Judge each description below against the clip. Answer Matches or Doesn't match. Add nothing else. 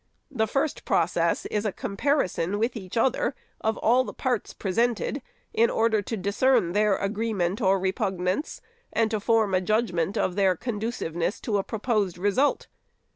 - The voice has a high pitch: Matches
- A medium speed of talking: Matches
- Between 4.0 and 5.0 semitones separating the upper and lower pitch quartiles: Doesn't match